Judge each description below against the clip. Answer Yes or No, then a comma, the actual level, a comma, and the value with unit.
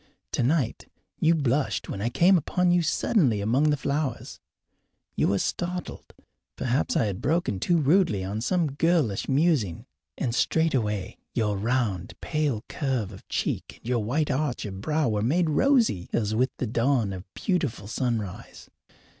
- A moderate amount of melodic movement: No, wide, 6.8 semitones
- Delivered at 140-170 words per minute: Yes, average, 155 wpm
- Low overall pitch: Yes, low, 130 Hz